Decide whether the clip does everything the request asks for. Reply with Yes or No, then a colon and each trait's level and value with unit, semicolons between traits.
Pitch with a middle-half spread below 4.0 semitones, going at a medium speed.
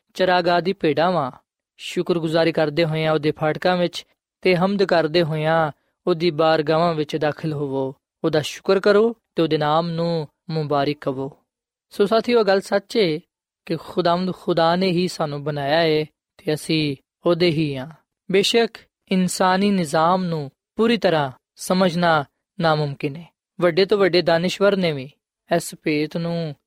Yes: average, 2.8 semitones; average, 140 wpm